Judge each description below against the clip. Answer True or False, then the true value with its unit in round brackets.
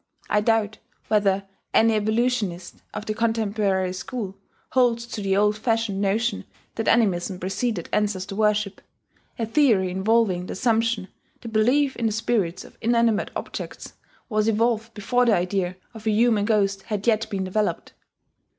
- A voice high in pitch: True (215 Hz)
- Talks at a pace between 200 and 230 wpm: False (150 wpm)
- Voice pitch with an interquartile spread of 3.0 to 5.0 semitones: False (2.6 semitones)